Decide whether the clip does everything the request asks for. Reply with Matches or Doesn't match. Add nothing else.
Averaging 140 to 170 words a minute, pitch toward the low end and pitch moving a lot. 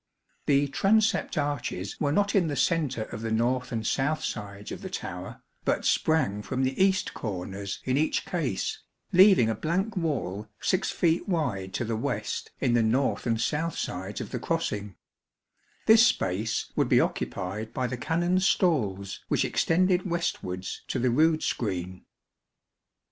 Matches